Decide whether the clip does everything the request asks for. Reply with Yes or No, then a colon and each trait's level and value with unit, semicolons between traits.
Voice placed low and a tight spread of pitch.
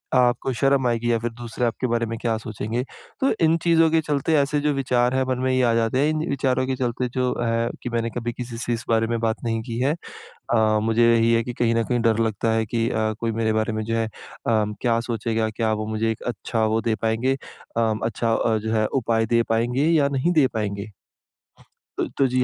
Yes: low, 115 Hz; narrow, 2.2 semitones